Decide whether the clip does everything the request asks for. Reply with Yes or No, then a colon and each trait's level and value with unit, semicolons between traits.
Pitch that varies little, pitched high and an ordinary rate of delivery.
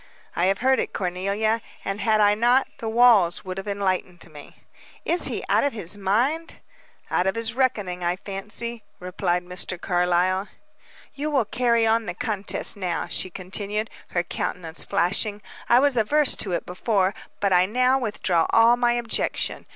No: average, 4.2 semitones; high, 205 Hz; average, 165 wpm